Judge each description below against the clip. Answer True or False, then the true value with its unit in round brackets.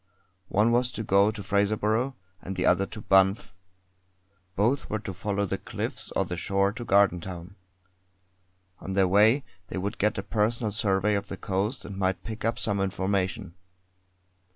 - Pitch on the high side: False (100 Hz)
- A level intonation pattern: True (2.0 semitones)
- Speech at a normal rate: True (165 wpm)